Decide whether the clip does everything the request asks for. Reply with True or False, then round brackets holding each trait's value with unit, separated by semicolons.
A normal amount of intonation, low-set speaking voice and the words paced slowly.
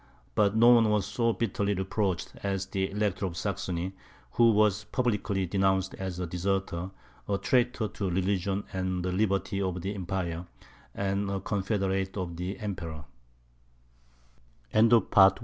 False (1.8 semitones; 95 Hz; 125 wpm)